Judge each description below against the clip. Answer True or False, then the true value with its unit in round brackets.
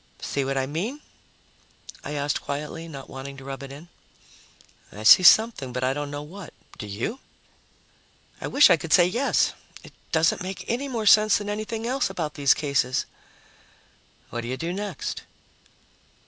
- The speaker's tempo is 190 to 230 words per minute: False (170 wpm)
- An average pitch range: False (7.1 semitones)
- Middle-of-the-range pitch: True (155 Hz)